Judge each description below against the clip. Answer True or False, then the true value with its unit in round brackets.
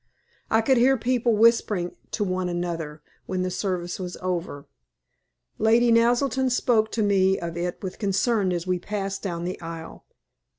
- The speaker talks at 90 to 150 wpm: False (160 wpm)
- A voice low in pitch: False (190 Hz)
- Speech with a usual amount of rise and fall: True (4.5 semitones)